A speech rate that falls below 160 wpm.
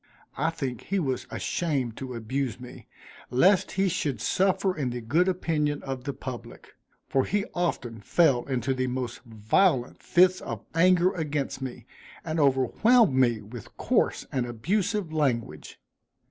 Yes: average, 145 wpm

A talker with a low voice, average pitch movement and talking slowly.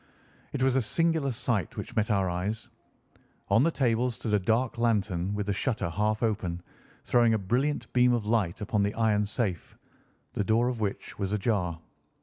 No: low, 110 Hz; average, 3.3 semitones; average, 180 wpm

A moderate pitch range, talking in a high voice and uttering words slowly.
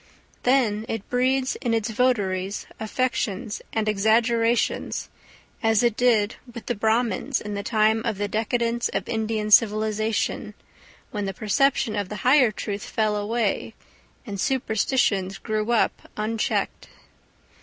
No: narrow, 2.3 semitones; high, 220 Hz; slow, 130 wpm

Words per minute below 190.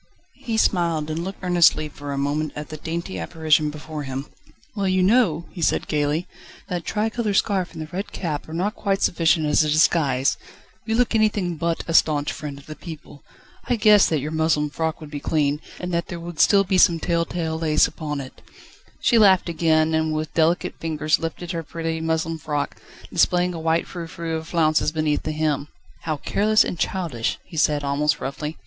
No: average, 200 wpm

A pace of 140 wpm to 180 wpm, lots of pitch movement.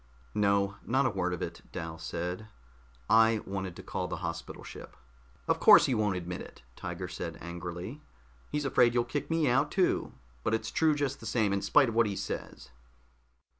No: average, 190 wpm; wide, 5.8 semitones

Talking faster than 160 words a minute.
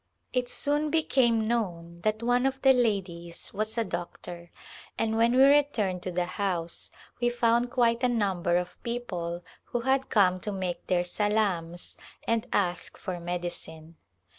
No: average, 155 wpm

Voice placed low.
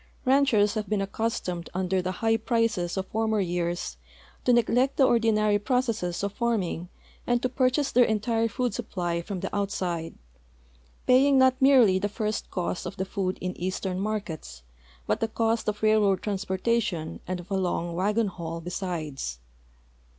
No: high, 205 Hz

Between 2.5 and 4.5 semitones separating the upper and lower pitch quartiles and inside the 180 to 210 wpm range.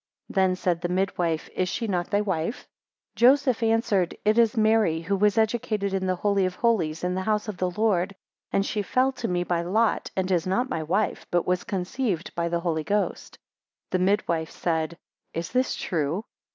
Yes: average, 3.6 semitones; fast, 205 wpm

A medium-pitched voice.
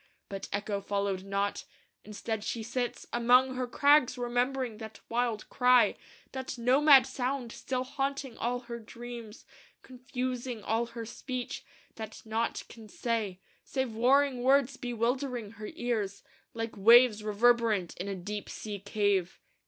No: high, 235 Hz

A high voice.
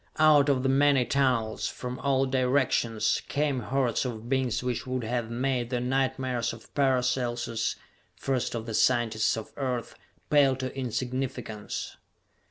No: low, 125 Hz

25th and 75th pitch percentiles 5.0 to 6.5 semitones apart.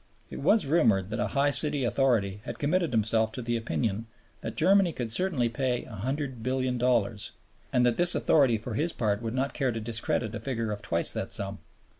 No: average, 3.7 semitones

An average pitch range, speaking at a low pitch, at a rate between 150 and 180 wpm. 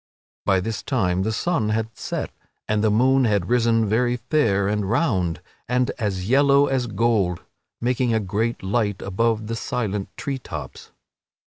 Yes: average, 3.5 semitones; low, 110 Hz; average, 155 wpm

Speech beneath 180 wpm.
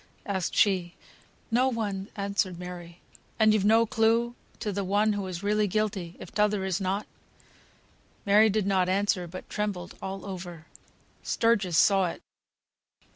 Yes: average, 145 wpm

